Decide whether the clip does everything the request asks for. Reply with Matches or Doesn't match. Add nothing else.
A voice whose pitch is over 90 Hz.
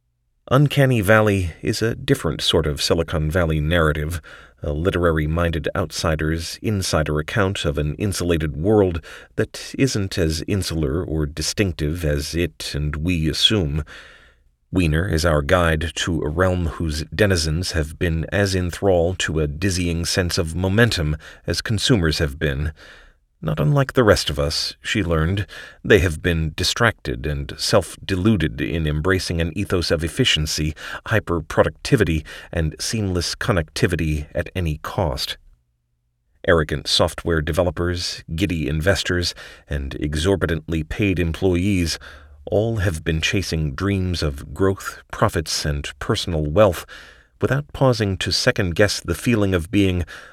Doesn't match